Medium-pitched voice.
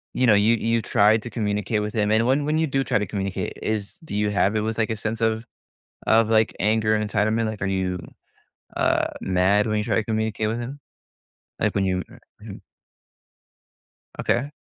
No: low, 110 Hz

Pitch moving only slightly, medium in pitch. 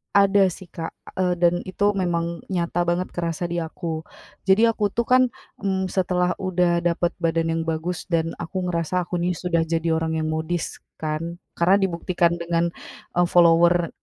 Yes: narrow, 1.6 semitones; medium, 175 Hz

